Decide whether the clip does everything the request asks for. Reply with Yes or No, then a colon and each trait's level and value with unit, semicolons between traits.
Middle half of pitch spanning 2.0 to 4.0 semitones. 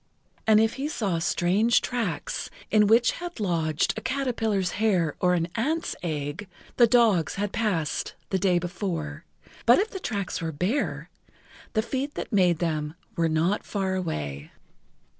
No: average, 5.3 semitones